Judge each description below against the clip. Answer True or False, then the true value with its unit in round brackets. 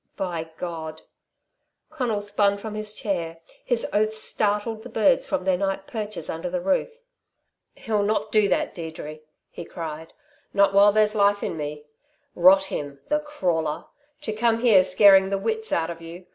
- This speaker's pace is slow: False (170 wpm)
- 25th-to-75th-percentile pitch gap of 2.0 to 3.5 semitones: False (4.1 semitones)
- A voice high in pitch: True (200 Hz)